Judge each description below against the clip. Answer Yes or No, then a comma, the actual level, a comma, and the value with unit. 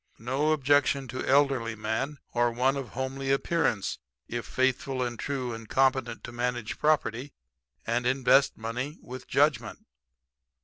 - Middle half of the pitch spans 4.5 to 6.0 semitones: No, narrow, 2.4 semitones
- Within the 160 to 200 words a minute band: No, slow, 135 wpm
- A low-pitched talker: Yes, low, 130 Hz